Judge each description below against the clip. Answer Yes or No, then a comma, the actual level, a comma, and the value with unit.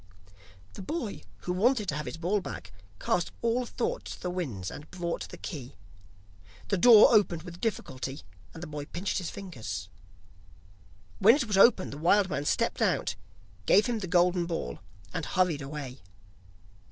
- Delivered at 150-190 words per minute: Yes, average, 165 wpm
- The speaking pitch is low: No, medium, 180 Hz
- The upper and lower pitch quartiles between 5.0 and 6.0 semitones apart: Yes, wide, 5.6 semitones